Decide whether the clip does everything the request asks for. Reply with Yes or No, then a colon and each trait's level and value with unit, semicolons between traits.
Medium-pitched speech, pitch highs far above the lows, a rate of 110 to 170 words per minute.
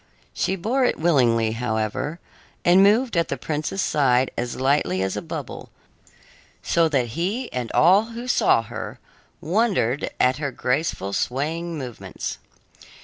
Yes: medium, 145 Hz; wide, 6.5 semitones; average, 140 wpm